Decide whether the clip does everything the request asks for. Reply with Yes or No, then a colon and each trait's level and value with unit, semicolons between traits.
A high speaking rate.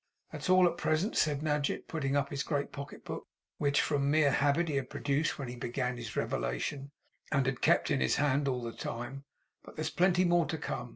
Yes: fast, 215 wpm